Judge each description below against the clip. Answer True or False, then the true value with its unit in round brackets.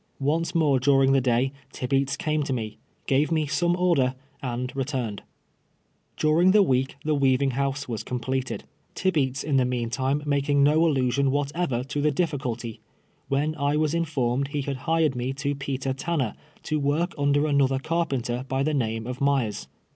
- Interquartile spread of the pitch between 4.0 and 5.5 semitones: False (2.6 semitones)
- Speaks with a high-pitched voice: False (140 Hz)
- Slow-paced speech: False (175 wpm)